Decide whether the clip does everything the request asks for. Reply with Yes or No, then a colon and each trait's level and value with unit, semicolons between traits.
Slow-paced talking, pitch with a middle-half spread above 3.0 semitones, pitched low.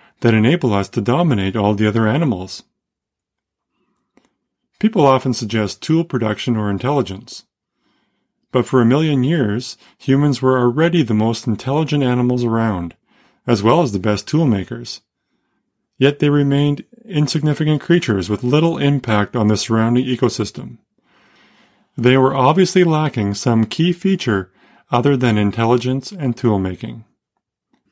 Yes: slow, 130 wpm; average, 5.0 semitones; low, 125 Hz